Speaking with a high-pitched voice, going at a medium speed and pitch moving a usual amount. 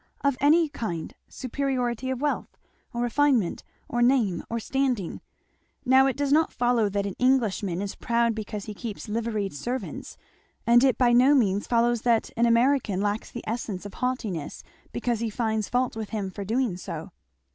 Yes: high, 235 Hz; average, 170 wpm; average, 3.6 semitones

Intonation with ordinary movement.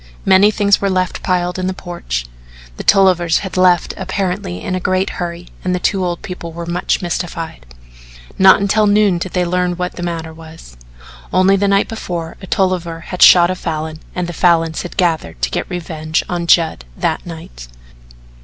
No: narrow, 2.1 semitones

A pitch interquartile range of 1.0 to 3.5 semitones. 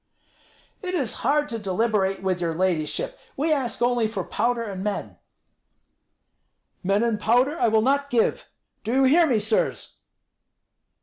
No: average, 4.9 semitones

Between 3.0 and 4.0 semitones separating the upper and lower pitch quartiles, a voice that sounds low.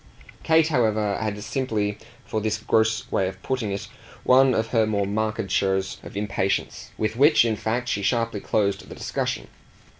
No: narrow, 2.5 semitones; low, 110 Hz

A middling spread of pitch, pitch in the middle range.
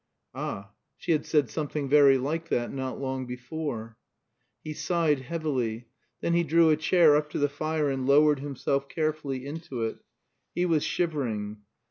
Yes: average, 3.3 semitones; medium, 145 Hz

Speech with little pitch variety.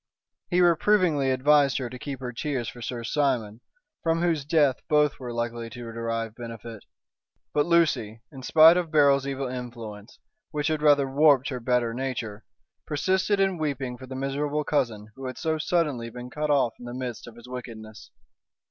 No: average, 4.0 semitones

